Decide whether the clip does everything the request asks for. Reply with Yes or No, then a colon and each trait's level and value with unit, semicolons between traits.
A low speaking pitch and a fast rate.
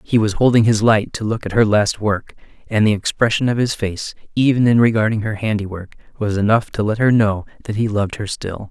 Yes: low, 110 Hz; fast, 225 wpm